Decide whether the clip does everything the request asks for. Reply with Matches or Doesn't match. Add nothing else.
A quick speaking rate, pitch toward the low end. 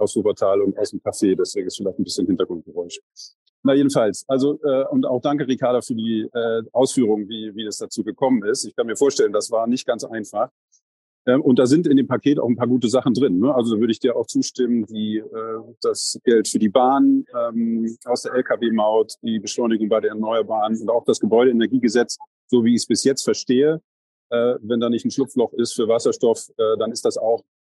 Matches